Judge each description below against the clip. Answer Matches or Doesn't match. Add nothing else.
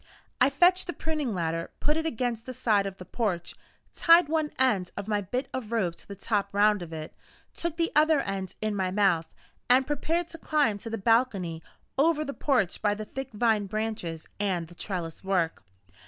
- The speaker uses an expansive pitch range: Matches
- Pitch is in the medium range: Doesn't match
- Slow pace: Doesn't match